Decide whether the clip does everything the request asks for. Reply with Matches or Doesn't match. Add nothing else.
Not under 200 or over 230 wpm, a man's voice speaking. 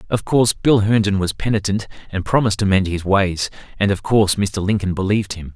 Matches